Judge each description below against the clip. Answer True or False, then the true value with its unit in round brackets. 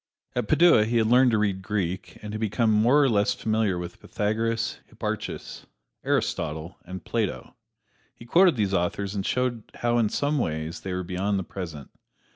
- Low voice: True (105 Hz)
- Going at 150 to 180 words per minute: True (175 wpm)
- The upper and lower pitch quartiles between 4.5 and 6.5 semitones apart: False (3.9 semitones)